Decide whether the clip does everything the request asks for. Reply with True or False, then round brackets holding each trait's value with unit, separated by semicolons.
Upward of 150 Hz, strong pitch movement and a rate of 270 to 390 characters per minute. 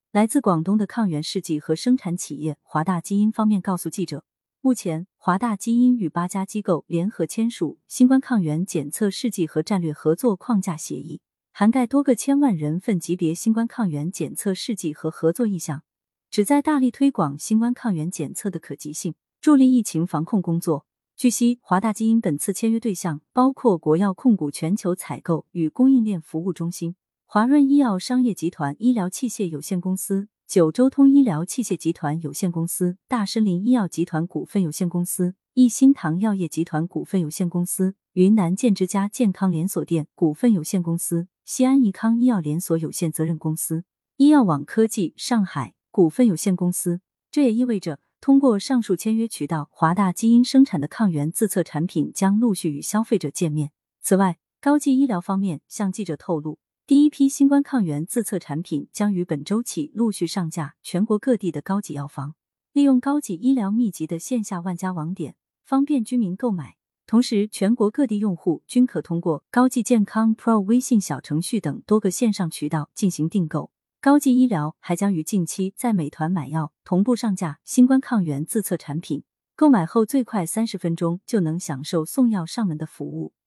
True (190 Hz; 6.1 semitones; 295 characters per minute)